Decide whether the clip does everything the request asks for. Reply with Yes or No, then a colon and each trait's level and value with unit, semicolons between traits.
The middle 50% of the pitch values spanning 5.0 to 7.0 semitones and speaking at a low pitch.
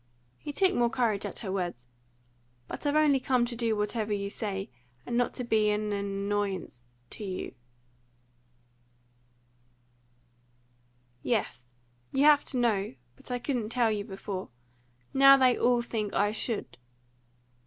No: wide, 5.6 semitones; high, 210 Hz